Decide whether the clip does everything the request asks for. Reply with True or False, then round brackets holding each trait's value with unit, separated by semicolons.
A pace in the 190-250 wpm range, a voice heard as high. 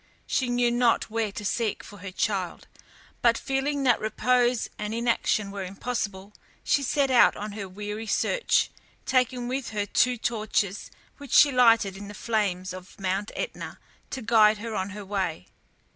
False (165 wpm; 220 Hz)